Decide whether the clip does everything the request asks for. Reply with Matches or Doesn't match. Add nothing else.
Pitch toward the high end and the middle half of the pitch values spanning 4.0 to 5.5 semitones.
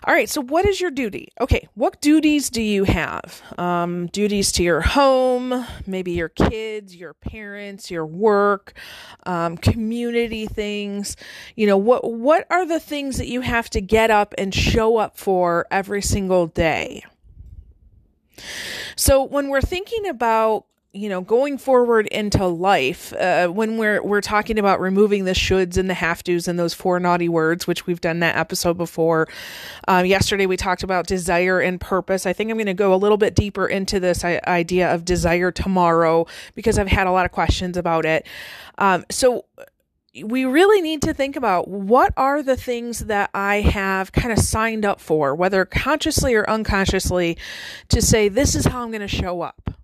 Matches